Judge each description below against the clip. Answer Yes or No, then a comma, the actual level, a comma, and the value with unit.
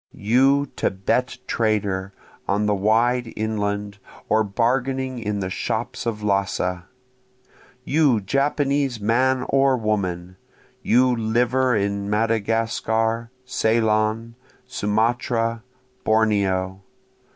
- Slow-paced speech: Yes, slow, 90 wpm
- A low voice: Yes, low, 110 Hz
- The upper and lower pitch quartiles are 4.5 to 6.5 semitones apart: No, average, 3.2 semitones